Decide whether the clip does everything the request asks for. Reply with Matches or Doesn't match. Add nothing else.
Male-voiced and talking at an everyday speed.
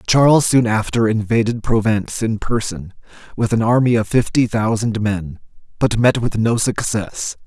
Matches